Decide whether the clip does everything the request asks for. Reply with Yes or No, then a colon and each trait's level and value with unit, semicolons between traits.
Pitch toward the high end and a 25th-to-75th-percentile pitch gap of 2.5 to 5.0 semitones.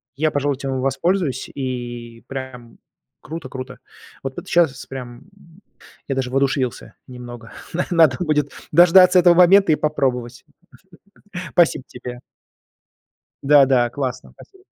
No: low, 135 Hz; average, 4.1 semitones